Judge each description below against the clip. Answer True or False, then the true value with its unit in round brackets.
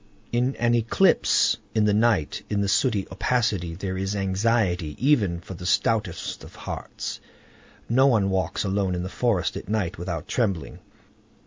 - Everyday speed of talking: True (155 wpm)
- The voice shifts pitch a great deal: False (4.0 semitones)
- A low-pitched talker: True (100 Hz)